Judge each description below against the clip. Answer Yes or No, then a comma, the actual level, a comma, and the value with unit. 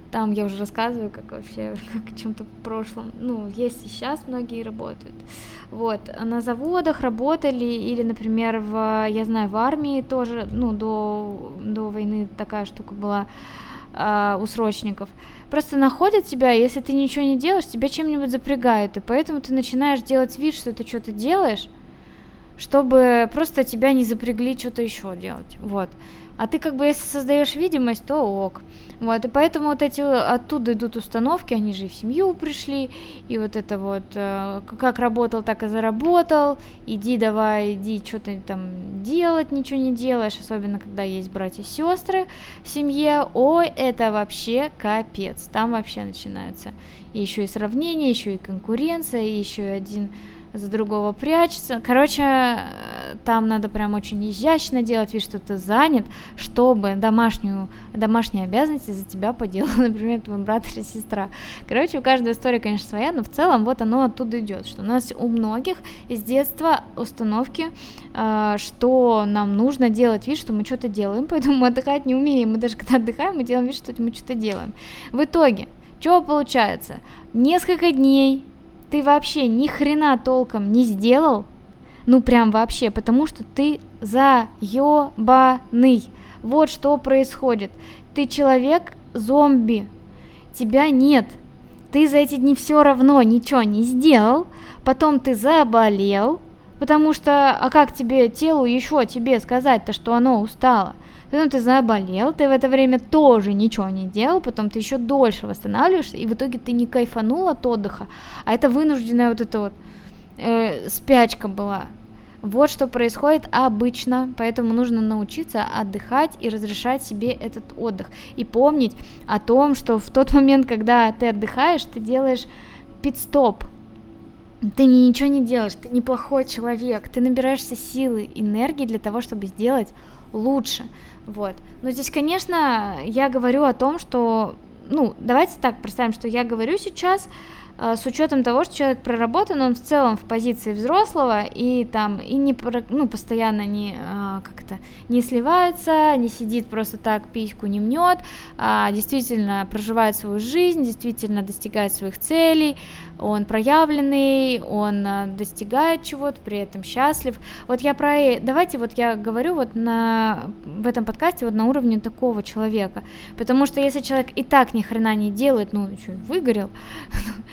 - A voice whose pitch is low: No, high, 240 Hz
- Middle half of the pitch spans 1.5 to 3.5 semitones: No, average, 4.1 semitones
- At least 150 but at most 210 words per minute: Yes, average, 155 wpm